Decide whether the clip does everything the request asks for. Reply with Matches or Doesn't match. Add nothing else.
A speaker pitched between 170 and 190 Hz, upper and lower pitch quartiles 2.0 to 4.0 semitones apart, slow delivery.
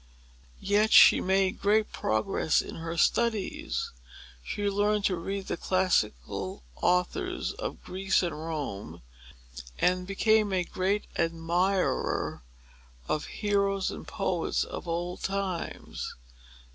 Matches